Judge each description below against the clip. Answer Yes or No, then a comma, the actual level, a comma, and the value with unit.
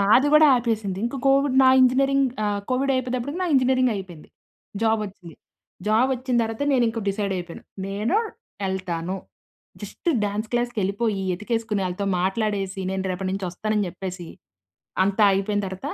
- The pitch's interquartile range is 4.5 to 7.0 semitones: Yes, average, 4.8 semitones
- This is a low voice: No, high, 215 Hz